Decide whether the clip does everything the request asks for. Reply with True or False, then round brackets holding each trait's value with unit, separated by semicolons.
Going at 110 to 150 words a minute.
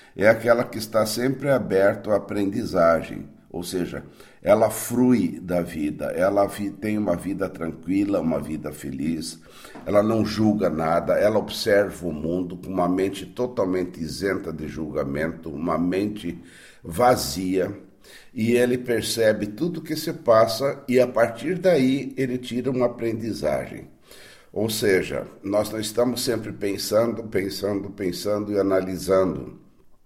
True (135 wpm)